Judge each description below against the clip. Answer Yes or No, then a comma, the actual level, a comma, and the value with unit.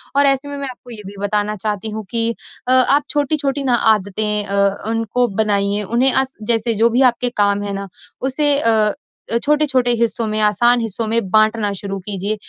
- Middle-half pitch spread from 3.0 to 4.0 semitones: Yes, average, 3.7 semitones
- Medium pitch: No, high, 225 Hz